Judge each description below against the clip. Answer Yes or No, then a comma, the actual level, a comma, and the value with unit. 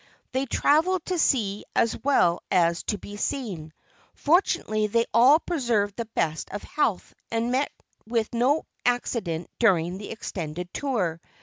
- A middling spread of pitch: No, wide, 6.1 semitones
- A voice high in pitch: Yes, high, 225 Hz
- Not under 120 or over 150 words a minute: Yes, average, 140 wpm